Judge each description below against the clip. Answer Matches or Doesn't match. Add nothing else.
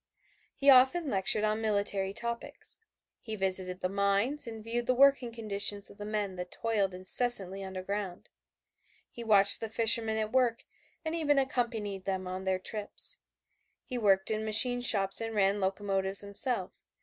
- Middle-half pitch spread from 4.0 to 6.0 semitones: Doesn't match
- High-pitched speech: Matches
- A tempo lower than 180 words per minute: Matches